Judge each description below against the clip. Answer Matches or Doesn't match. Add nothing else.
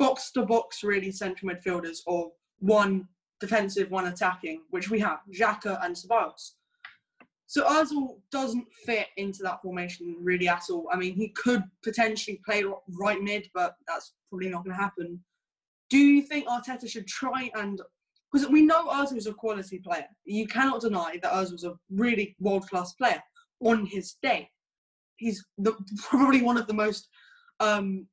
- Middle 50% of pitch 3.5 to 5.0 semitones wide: Matches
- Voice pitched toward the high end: Matches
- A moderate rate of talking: Matches